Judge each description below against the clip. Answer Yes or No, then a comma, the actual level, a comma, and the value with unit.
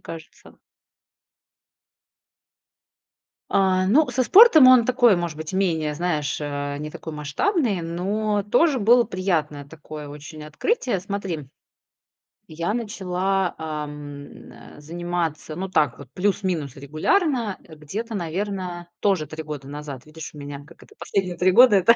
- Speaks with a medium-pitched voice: Yes, medium, 175 Hz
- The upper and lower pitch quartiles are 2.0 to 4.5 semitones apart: No, average, 5.2 semitones